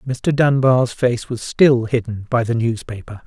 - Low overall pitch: Yes, low, 120 Hz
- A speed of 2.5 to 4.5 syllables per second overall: Yes, 4.2 syllables/s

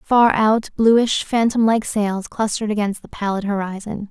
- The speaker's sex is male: No, female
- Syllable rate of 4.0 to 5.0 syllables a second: Yes, 4.5 syllables/s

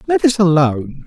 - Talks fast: No, average, 170 wpm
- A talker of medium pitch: Yes, medium, 155 Hz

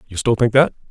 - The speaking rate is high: Yes, fast, 265 wpm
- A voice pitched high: No, low, 120 Hz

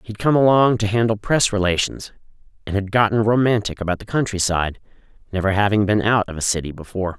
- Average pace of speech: Yes, average, 185 wpm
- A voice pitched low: Yes, low, 105 Hz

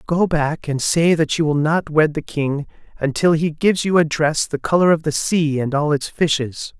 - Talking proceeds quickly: Yes, fast, 230 wpm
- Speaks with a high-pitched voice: No, medium, 155 Hz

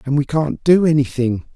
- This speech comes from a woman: No, male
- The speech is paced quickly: No, average, 195 wpm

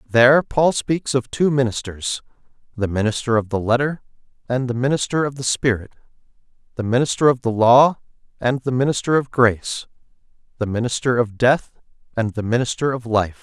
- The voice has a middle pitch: No, low, 125 Hz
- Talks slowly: No, average, 160 wpm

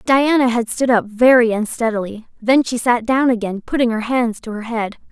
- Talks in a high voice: Yes, high, 235 Hz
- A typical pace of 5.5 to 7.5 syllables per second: No, 5.0 syllables/s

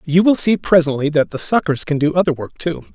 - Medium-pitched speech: Yes, medium, 160 Hz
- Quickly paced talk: Yes, fast, 245 wpm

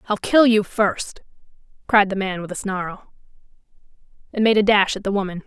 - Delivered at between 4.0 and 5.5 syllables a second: Yes, 5.2 syllables/s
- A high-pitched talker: Yes, high, 200 Hz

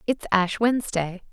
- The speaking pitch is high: Yes, high, 205 Hz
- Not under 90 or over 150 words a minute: Yes, slow, 135 wpm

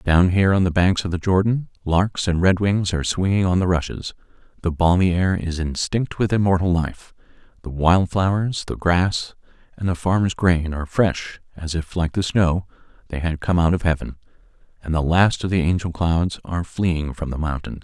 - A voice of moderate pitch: No, very low, 90 Hz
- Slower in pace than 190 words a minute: No, average, 195 wpm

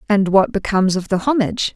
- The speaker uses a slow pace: No, fast, 205 wpm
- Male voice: No, female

